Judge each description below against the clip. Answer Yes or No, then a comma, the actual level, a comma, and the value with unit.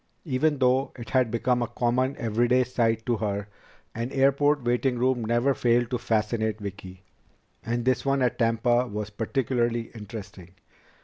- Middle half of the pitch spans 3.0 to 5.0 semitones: No, narrow, 2.4 semitones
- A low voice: Yes, low, 120 Hz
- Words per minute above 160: No, average, 150 wpm